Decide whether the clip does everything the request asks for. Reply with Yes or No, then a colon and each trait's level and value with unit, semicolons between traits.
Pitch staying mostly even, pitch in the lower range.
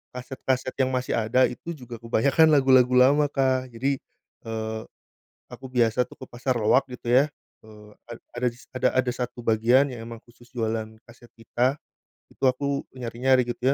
Yes: narrow, 1.9 semitones; low, 125 Hz